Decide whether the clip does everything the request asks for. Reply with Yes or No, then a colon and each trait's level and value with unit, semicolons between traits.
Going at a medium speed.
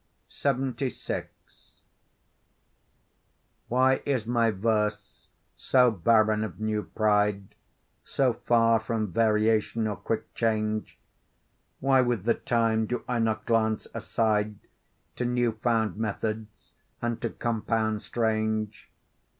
No: slow, 105 wpm